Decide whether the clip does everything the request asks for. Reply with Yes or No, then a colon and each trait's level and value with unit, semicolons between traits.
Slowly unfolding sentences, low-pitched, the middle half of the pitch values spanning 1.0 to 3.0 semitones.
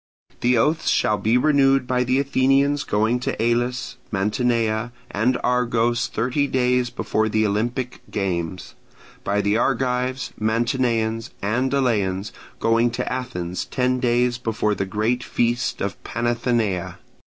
Yes: slow, 130 wpm; low, 120 Hz; average, 2.7 semitones